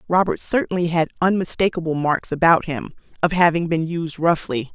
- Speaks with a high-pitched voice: No, medium, 170 Hz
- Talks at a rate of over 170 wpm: No, average, 150 wpm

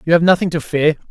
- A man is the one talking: Yes, male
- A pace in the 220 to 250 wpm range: No, fast, 270 wpm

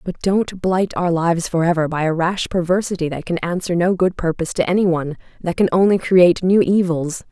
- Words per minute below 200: No, fast, 205 wpm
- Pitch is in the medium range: Yes, medium, 175 Hz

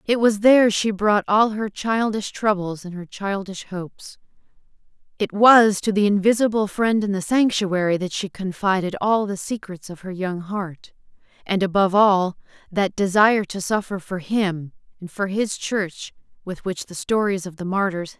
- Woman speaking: Yes, female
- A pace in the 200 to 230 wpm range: No, average, 180 wpm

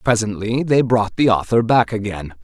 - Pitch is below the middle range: Yes, low, 110 Hz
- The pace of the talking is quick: No, average, 175 wpm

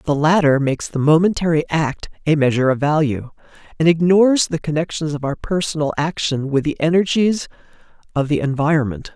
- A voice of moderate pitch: Yes, medium, 155 Hz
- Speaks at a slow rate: No, average, 155 wpm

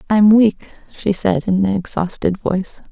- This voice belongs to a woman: Yes, female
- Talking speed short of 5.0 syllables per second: Yes, 4.5 syllables/s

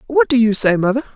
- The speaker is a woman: Yes, female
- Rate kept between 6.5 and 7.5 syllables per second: Yes, 6.9 syllables/s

